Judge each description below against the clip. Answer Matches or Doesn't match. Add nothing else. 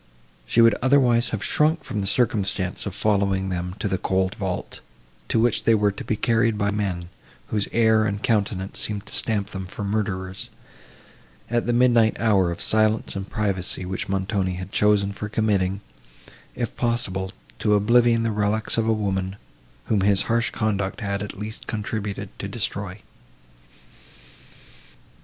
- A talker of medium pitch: Doesn't match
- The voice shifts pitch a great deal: Doesn't match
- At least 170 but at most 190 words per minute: Doesn't match